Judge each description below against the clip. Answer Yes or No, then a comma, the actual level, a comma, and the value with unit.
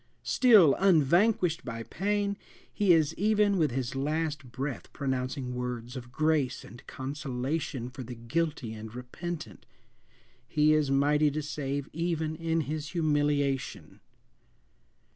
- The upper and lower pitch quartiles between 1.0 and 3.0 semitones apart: No, average, 4.2 semitones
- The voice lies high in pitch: No, medium, 145 Hz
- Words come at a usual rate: No, slow, 125 wpm